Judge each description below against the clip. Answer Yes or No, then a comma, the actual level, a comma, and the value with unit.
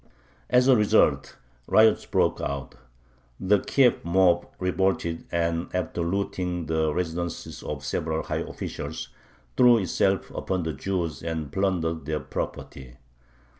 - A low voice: Yes, very low, 85 Hz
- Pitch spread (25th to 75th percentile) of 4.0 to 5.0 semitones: No, average, 2.9 semitones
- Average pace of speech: No, slow, 125 wpm